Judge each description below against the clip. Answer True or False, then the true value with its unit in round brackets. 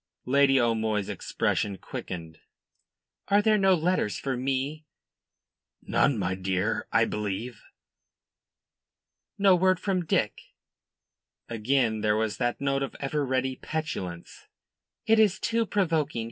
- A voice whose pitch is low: True (130 Hz)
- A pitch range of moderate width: False (7.5 semitones)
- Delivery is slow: True (120 wpm)